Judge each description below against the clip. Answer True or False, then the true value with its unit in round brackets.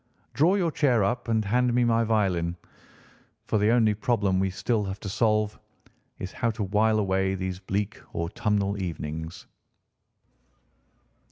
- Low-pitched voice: True (105 Hz)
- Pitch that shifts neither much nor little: True (3.3 semitones)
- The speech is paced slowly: False (145 wpm)